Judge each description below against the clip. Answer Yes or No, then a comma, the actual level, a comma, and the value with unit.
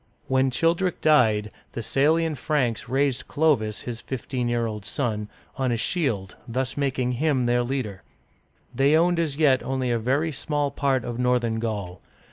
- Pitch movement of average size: Yes, average, 3.7 semitones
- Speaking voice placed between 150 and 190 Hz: No, low, 130 Hz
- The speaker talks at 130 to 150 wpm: No, average, 160 wpm